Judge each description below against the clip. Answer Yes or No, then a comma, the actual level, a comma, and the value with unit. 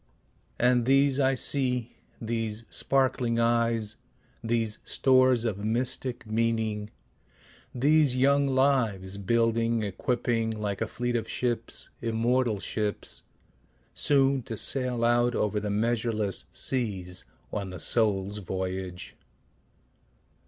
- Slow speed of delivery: Yes, slow, 105 wpm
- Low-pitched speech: Yes, low, 115 Hz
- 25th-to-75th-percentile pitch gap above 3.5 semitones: No, average, 3.0 semitones